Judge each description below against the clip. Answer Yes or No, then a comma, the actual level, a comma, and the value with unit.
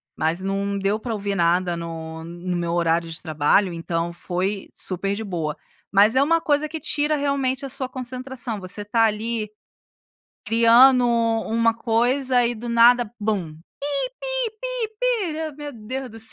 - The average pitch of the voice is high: Yes, high, 225 Hz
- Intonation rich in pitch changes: Yes, wide, 6.2 semitones